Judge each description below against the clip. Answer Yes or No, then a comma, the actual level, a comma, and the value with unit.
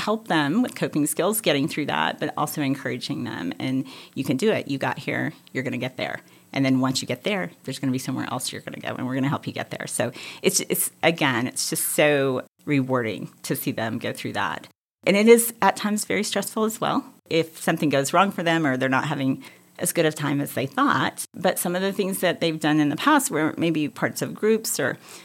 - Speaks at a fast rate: Yes, fast, 240 wpm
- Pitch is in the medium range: Yes, medium, 155 Hz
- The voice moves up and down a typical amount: No, wide, 6.5 semitones